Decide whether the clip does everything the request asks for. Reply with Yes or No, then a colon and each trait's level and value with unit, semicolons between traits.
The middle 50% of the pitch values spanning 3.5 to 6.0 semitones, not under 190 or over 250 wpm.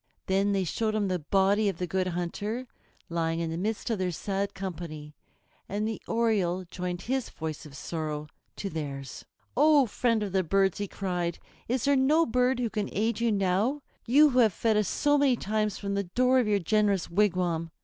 Yes: average, 4.4 semitones; average, 200 wpm